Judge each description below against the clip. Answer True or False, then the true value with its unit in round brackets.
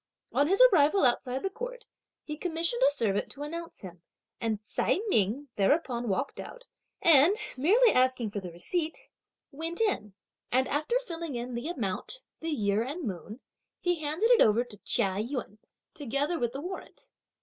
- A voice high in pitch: True (280 Hz)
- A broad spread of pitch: True (6.9 semitones)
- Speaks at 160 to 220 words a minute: True (165 wpm)